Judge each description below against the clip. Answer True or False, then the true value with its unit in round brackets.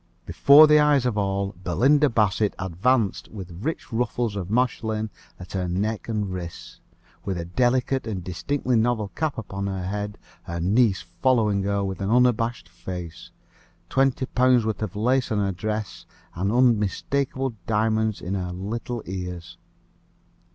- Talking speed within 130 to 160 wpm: True (150 wpm)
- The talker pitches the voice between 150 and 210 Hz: False (105 Hz)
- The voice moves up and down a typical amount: True (4.4 semitones)